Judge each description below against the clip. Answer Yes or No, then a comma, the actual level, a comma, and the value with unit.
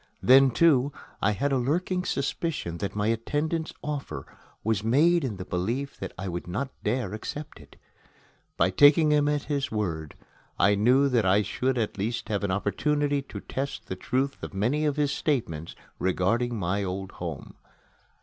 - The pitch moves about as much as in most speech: No, wide, 6.6 semitones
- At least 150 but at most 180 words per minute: Yes, average, 170 wpm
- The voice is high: No, low, 120 Hz